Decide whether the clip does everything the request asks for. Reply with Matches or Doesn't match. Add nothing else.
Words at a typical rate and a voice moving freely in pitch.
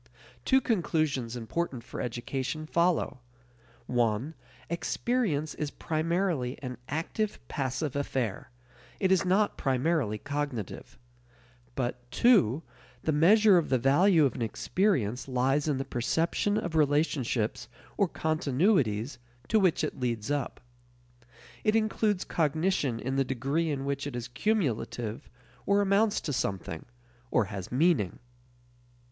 Doesn't match